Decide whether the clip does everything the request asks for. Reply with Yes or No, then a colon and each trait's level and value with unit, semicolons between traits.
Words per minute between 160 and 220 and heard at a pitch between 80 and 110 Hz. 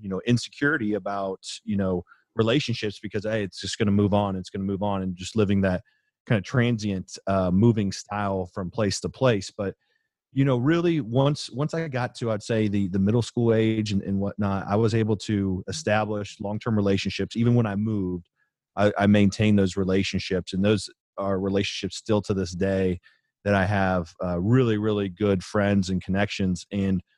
Yes: average, 195 wpm; low, 100 Hz